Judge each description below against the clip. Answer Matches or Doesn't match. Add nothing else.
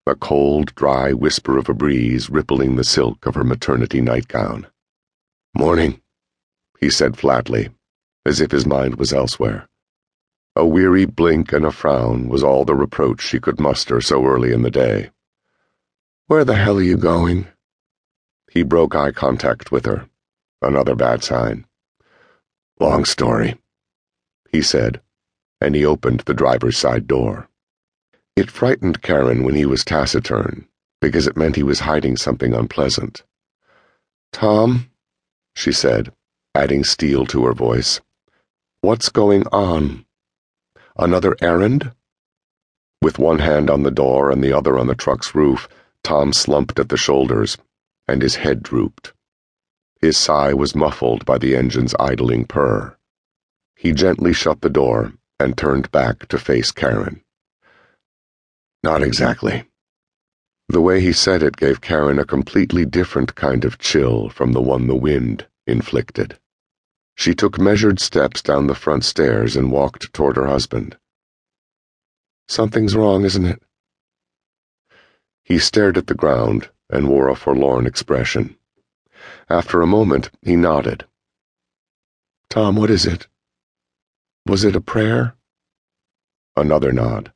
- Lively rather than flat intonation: Matches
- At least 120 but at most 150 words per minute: Matches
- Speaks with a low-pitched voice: Matches